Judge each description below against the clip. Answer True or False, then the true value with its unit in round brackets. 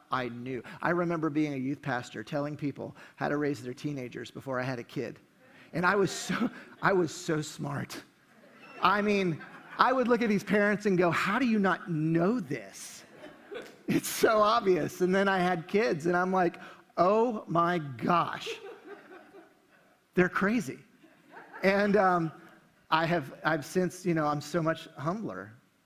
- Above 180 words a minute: False (165 wpm)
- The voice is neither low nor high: True (175 Hz)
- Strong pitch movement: False (4.7 semitones)